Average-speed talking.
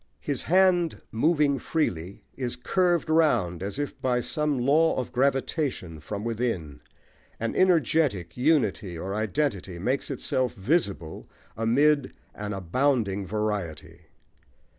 No: slow, 115 wpm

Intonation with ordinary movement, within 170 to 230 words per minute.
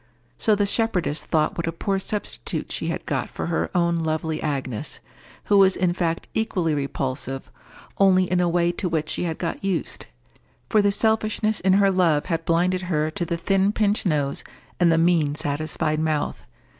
Yes: average, 3.7 semitones; average, 180 wpm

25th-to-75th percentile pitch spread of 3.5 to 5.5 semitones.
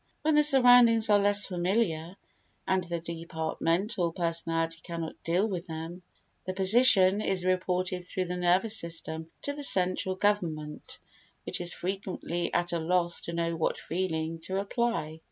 No: average, 3.0 semitones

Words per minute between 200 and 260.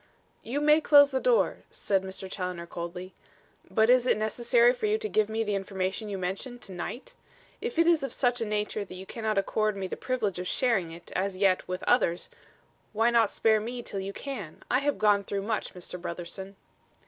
Yes: fast, 205 wpm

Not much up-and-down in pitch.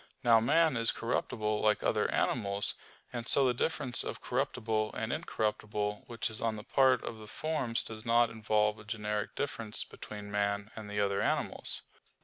Yes: narrow, 2.1 semitones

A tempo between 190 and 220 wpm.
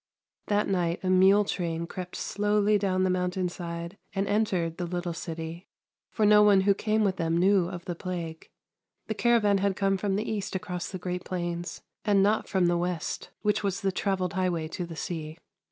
Yes: average, 200 wpm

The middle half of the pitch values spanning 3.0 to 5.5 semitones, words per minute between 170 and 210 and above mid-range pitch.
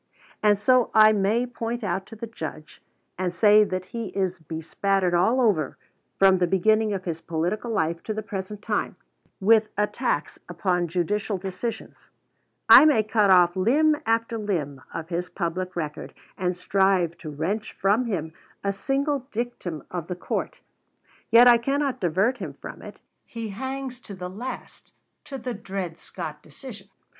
No: average, 4.4 semitones; average, 160 wpm; high, 200 Hz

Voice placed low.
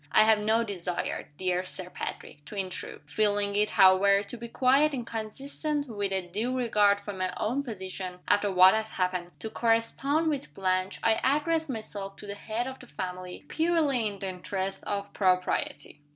No: high, 205 Hz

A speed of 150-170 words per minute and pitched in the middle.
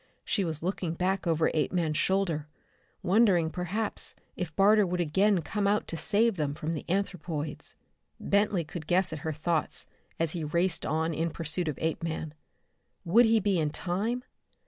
Yes: average, 165 wpm; medium, 175 Hz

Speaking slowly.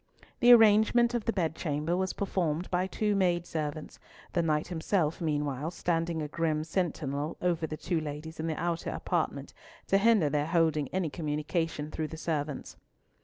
No: average, 165 wpm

